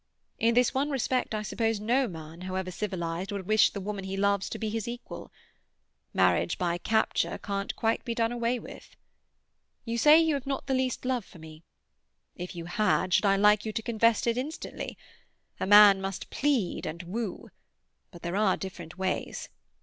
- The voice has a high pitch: Yes, high, 210 Hz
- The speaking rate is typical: Yes, average, 185 wpm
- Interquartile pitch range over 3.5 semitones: Yes, average, 4.0 semitones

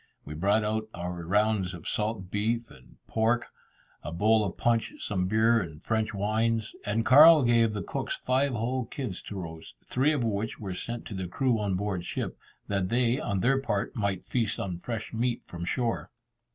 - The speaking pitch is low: Yes, low, 110 Hz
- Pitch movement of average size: Yes, average, 3.6 semitones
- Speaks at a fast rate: No, average, 190 wpm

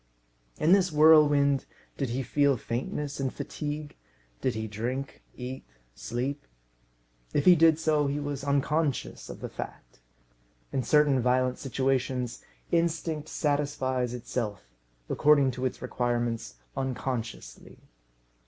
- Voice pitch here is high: No, low, 135 Hz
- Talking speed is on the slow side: Yes, slow, 115 wpm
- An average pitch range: Yes, average, 3.0 semitones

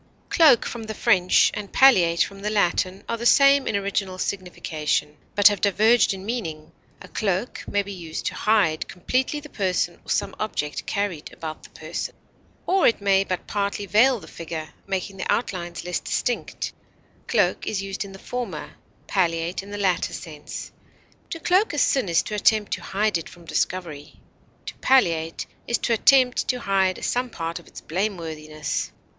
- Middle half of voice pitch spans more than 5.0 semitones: No, average, 4.4 semitones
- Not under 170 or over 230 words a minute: Yes, average, 175 wpm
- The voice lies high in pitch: Yes, high, 195 Hz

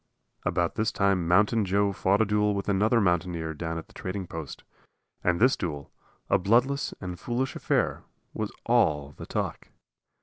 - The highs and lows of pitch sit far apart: No, average, 3.5 semitones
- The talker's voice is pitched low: Yes, very low, 95 Hz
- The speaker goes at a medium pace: Yes, average, 165 wpm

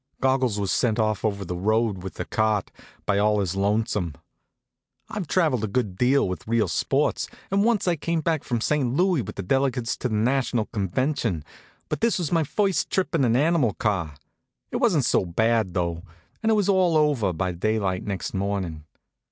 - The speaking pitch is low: Yes, low, 115 Hz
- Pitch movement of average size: No, wide, 6.8 semitones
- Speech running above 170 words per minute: Yes, average, 190 wpm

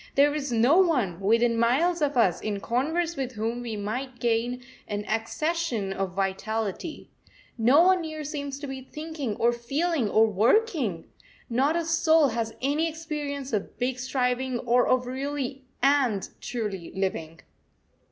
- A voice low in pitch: No, very high, 250 Hz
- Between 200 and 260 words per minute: No, average, 150 wpm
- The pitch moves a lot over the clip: No, average, 4.9 semitones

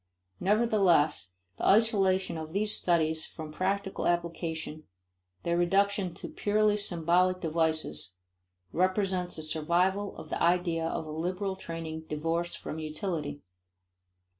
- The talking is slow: Yes, slow, 115 wpm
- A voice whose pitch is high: No, medium, 175 Hz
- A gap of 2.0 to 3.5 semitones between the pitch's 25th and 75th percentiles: Yes, average, 3.2 semitones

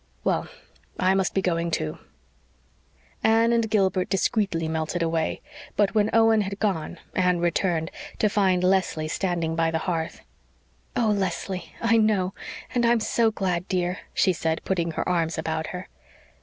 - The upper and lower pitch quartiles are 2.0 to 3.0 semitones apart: No, average, 3.8 semitones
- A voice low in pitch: No, medium, 185 Hz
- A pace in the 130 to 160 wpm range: Yes, average, 155 wpm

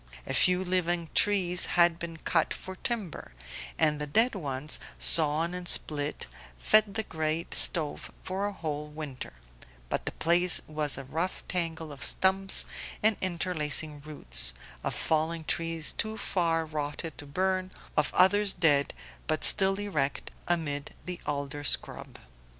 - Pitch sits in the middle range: Yes, medium, 165 Hz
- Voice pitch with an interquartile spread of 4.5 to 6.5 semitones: No, average, 3.7 semitones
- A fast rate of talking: No, average, 145 wpm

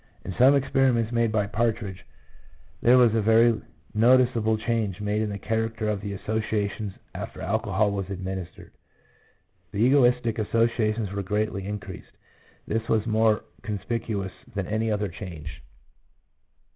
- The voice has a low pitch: Yes, low, 110 Hz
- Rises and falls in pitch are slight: Yes, narrow, 2.3 semitones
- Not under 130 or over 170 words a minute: Yes, slow, 135 wpm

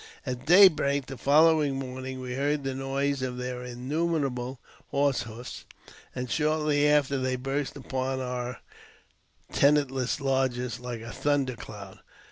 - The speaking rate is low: Yes, slow, 130 wpm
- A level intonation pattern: Yes, narrow, 2.3 semitones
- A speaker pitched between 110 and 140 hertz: Yes, low, 135 Hz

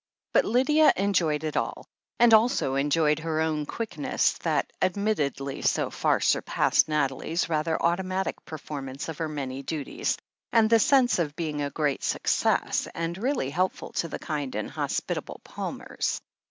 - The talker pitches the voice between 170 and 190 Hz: No, medium, 160 Hz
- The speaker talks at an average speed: Yes, average, 150 wpm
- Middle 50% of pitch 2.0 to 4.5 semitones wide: No, average, 5.0 semitones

